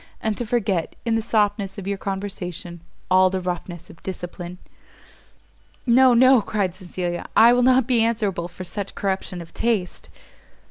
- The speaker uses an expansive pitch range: No, average, 4.1 semitones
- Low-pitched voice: No, high, 195 Hz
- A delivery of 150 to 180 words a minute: Yes, average, 155 wpm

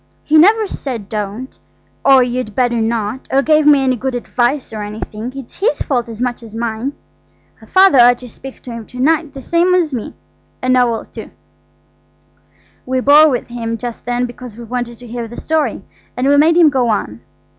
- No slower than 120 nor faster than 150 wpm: No, average, 190 wpm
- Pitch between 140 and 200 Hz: No, very high, 250 Hz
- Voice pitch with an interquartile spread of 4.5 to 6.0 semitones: No, average, 3.2 semitones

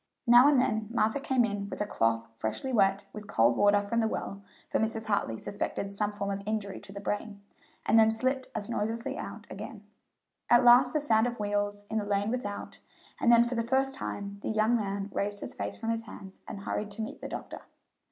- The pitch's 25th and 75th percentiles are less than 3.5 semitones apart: Yes, narrow, 2.5 semitones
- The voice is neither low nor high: No, high, 215 Hz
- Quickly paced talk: Yes, fast, 220 wpm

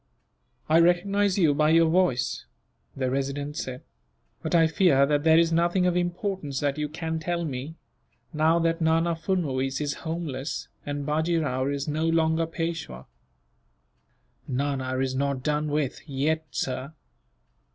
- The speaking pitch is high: No, medium, 155 Hz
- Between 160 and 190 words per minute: No, average, 145 wpm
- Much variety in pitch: No, average, 3.1 semitones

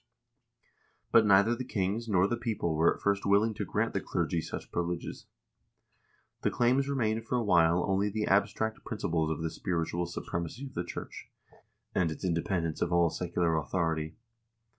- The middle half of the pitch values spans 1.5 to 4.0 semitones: No, average, 4.7 semitones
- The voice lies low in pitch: Yes, very low, 95 Hz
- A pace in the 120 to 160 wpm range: No, average, 175 wpm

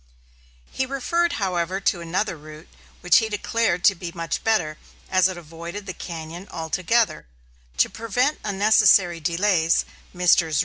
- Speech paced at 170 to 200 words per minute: No, average, 140 wpm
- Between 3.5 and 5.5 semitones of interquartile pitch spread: Yes, average, 3.9 semitones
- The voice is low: No, medium, 180 Hz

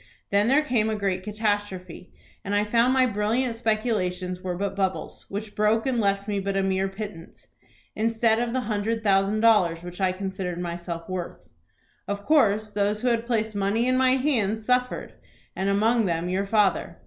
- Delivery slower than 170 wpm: No, average, 180 wpm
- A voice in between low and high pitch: No, high, 205 Hz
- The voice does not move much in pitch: No, average, 3.0 semitones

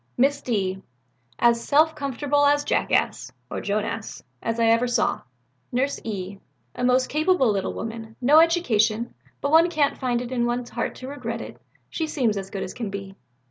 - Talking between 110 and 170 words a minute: No, average, 180 wpm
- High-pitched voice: Yes, high, 245 Hz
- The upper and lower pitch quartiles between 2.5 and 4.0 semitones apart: No, average, 4.4 semitones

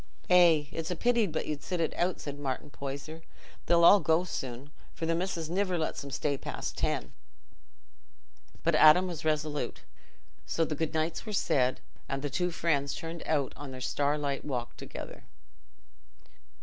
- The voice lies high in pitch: No, medium, 155 Hz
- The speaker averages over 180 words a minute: No, average, 165 wpm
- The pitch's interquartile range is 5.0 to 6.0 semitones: No, average, 3.2 semitones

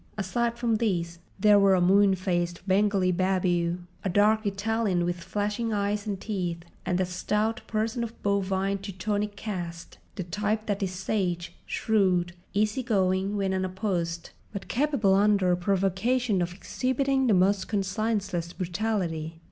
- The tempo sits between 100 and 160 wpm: Yes, average, 140 wpm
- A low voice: No, high, 195 Hz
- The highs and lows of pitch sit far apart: No, average, 2.8 semitones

